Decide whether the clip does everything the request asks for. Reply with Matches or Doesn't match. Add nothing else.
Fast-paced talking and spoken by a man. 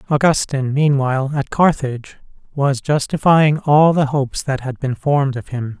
Doesn't match